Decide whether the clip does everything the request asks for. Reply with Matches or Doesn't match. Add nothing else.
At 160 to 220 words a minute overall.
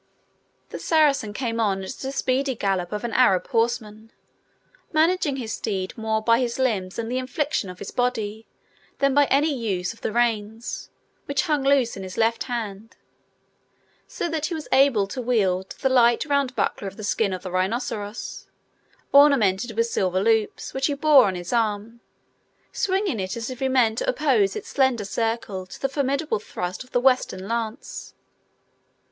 Matches